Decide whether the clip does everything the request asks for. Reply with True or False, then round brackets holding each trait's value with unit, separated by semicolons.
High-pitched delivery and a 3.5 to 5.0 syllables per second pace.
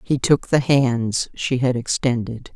False (125 Hz; 3.8 syllables/s)